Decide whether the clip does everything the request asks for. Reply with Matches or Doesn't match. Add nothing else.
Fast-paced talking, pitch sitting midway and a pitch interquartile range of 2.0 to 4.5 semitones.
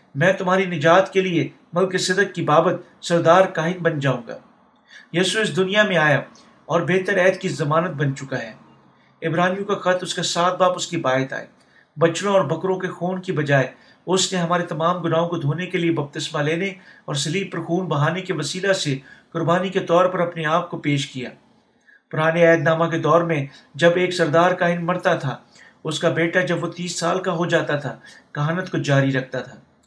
Matches